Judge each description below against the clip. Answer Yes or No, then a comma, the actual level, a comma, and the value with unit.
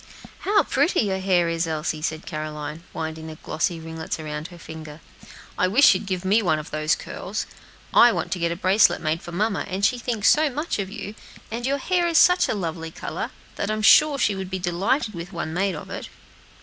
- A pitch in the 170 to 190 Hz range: Yes, medium, 185 Hz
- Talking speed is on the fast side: Yes, fast, 220 wpm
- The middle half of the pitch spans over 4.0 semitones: Yes, average, 5.2 semitones